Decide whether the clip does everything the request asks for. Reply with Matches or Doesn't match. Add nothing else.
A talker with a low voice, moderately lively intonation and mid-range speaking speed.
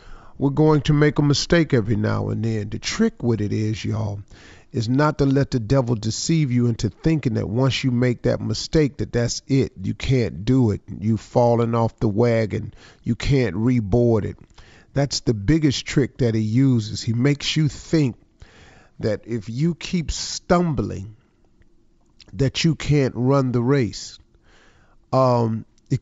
Matches